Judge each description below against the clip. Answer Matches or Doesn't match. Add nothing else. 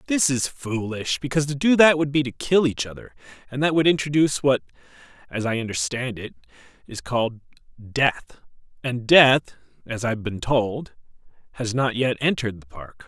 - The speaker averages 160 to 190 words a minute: Matches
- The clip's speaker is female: Doesn't match